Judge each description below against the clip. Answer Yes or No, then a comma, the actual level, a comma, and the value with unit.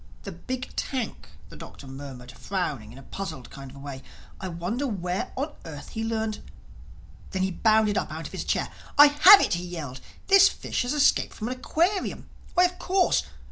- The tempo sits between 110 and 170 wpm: No, average, 190 wpm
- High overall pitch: Yes, high, 205 Hz